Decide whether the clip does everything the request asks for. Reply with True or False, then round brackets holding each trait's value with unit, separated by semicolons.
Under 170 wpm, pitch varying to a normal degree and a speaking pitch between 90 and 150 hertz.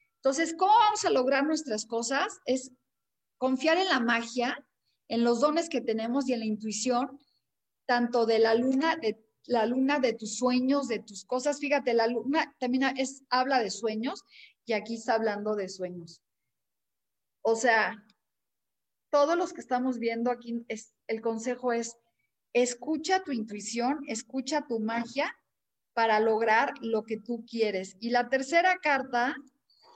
False (150 wpm; 3.5 semitones; 245 Hz)